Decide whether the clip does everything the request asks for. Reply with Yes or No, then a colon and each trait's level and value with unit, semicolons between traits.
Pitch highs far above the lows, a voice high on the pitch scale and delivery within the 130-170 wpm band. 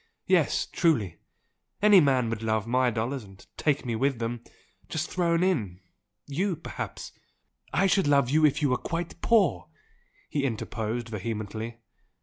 No: wide, 5.9 semitones; low, 130 Hz; average, 150 wpm